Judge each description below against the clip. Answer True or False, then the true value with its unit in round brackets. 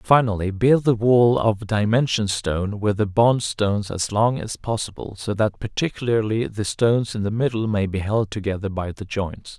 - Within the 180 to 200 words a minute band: True (190 wpm)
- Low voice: True (110 Hz)